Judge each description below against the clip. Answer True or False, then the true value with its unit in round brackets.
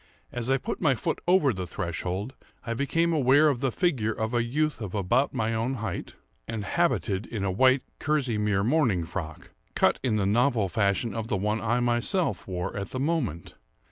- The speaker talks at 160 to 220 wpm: True (185 wpm)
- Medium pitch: False (115 Hz)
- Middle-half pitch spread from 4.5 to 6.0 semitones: True (5.0 semitones)